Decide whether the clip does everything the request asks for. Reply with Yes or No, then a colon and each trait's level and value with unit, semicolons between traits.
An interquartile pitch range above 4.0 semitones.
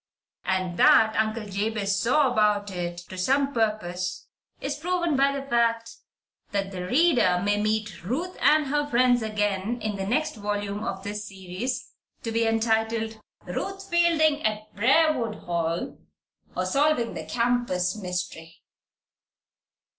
Yes: average, 4.6 semitones